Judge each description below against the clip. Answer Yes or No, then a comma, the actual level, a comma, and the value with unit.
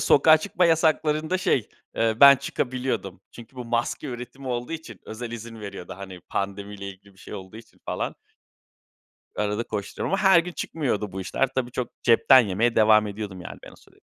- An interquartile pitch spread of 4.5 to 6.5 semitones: Yes, average, 5.0 semitones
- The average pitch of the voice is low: Yes, low, 115 Hz